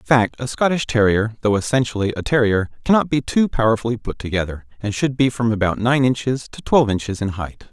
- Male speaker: Yes, male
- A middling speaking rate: No, fast, 210 wpm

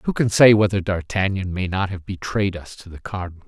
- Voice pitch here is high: No, very low, 95 Hz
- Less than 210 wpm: No, fast, 225 wpm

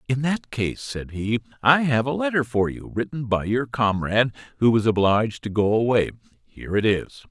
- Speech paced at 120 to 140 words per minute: No, average, 195 wpm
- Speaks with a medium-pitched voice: No, low, 115 Hz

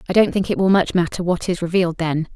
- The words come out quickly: Yes, fast, 280 wpm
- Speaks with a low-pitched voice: No, medium, 180 Hz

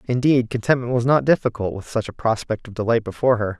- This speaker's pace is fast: Yes, fast, 215 wpm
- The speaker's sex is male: Yes, male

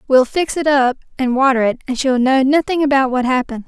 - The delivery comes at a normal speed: No, fast, 230 wpm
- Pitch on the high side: Yes, very high, 265 Hz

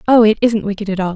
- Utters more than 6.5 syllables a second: Yes, 7.4 syllables/s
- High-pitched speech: Yes, high, 210 Hz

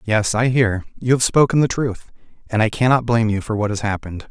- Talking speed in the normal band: No, fast, 235 wpm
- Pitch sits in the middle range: No, low, 115 Hz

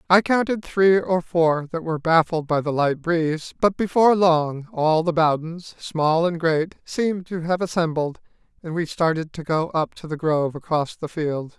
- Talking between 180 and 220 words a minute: Yes, average, 190 wpm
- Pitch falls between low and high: Yes, medium, 165 Hz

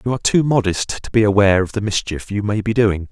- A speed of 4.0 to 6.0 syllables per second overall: No, 6.4 syllables/s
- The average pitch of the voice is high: No, low, 105 Hz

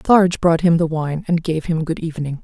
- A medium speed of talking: No, fast, 245 wpm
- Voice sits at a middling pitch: Yes, medium, 165 Hz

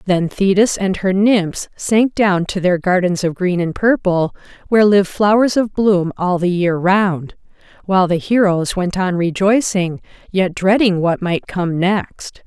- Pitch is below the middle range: No, high, 190 Hz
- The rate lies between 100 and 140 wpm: No, average, 170 wpm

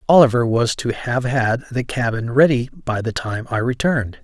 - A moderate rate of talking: Yes, average, 185 wpm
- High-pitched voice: No, low, 125 Hz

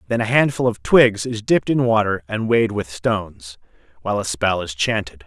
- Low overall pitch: Yes, low, 105 Hz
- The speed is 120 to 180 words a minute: No, fast, 205 wpm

